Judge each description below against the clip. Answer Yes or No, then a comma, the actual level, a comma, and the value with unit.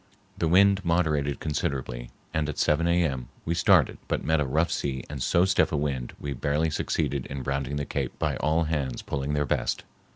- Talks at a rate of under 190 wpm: No, average, 195 wpm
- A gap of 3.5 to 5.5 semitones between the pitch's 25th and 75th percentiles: No, average, 3.0 semitones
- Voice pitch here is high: No, very low, 75 Hz